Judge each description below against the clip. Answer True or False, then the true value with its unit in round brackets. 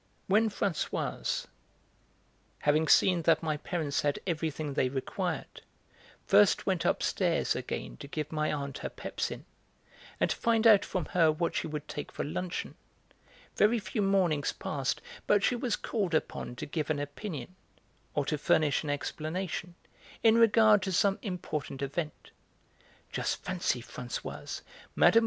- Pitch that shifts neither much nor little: True (4.9 semitones)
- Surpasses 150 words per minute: False (145 wpm)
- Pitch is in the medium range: True (160 Hz)